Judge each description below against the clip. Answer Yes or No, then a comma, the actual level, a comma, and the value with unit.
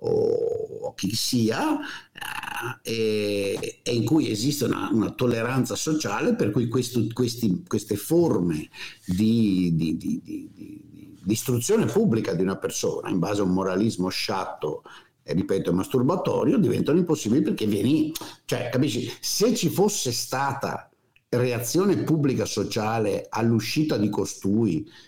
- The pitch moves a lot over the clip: Yes, wide, 7.1 semitones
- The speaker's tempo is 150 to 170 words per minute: No, average, 130 wpm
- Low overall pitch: Yes, low, 125 Hz